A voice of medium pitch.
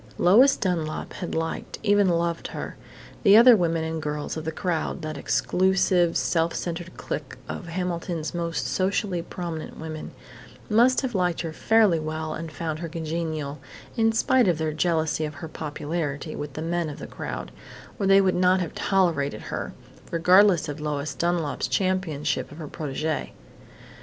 Yes: medium, 170 Hz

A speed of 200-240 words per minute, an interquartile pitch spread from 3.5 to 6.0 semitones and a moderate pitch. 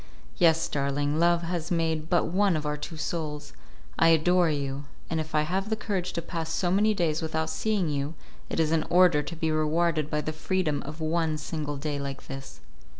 No: fast, 205 wpm; narrow, 2.4 semitones; medium, 160 Hz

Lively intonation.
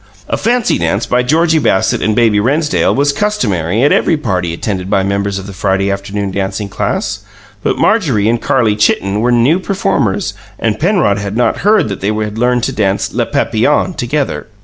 Yes: wide, 6.4 semitones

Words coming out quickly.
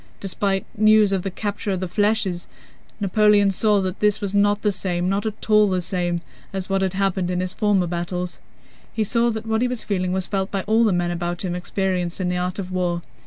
Yes: fast, 225 wpm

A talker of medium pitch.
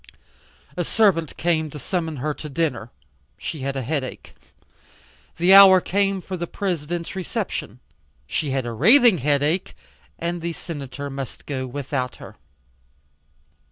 Yes: medium, 160 Hz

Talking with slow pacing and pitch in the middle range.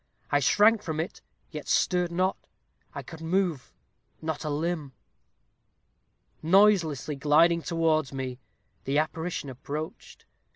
Yes: slow, 115 wpm; medium, 160 Hz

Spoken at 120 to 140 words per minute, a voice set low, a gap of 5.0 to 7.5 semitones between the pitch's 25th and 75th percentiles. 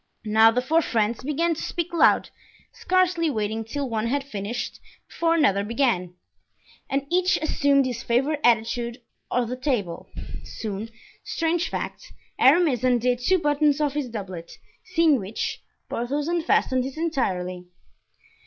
No: slow, 135 wpm; very high, 255 Hz; wide, 5.5 semitones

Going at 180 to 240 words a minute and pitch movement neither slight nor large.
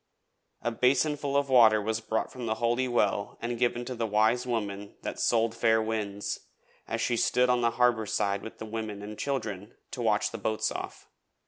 No: average, 195 wpm; narrow, 2.2 semitones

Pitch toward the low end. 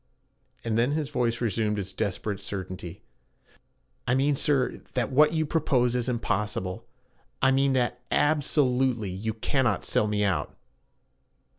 Yes: low, 120 Hz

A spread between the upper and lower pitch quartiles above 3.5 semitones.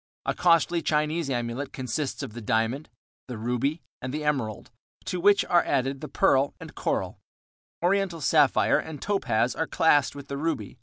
Yes: average, 4.5 semitones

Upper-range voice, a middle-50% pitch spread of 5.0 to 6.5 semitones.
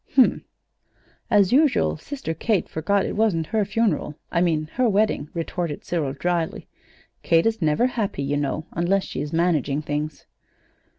No: medium, 170 Hz; wide, 5.6 semitones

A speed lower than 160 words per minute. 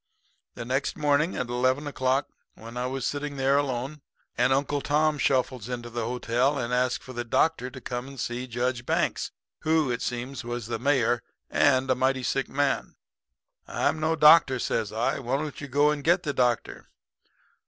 No: average, 185 wpm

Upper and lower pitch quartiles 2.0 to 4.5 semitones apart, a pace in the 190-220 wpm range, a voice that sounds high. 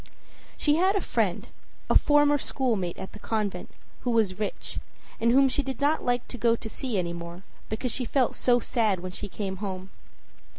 No: wide, 5.5 semitones; average, 195 wpm; high, 230 Hz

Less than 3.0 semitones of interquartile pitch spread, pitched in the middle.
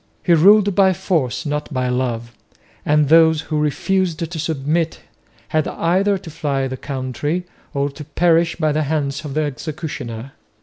No: average, 3.3 semitones; medium, 155 Hz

